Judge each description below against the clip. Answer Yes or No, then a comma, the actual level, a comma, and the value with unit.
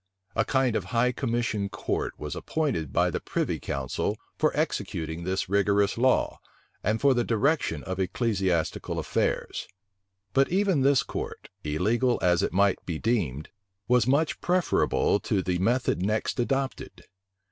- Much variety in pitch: Yes, wide, 5.8 semitones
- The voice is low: Yes, low, 110 Hz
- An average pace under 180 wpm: Yes, average, 145 wpm